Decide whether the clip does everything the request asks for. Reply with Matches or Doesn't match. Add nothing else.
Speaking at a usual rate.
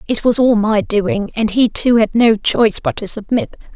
Doesn't match